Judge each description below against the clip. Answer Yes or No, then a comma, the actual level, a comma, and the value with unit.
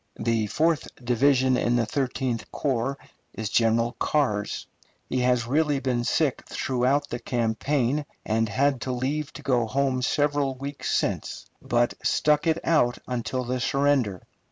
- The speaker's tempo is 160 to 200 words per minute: No, average, 140 wpm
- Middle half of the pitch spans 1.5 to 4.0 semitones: Yes, average, 3.0 semitones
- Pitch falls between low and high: No, low, 130 Hz